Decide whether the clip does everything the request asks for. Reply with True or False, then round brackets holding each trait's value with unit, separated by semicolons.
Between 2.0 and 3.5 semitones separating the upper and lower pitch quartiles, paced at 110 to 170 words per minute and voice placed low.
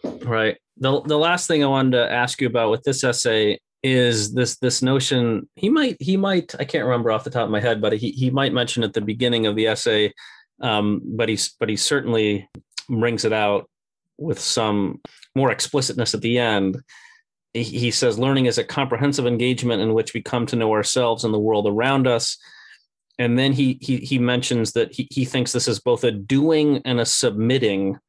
False (3.0 semitones; 205 wpm; 120 Hz)